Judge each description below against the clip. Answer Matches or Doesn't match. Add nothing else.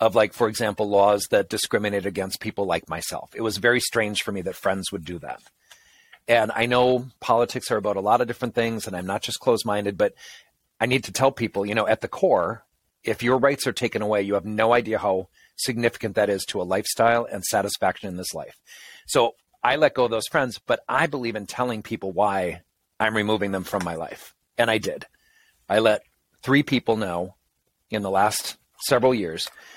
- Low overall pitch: Matches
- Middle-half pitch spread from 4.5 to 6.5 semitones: Doesn't match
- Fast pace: Matches